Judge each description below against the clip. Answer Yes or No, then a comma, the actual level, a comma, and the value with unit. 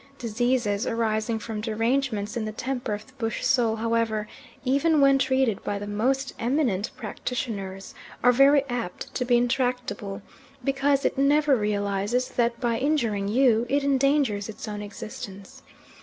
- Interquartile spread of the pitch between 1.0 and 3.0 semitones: No, average, 3.9 semitones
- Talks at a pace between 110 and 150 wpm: Yes, average, 145 wpm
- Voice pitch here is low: No, high, 235 Hz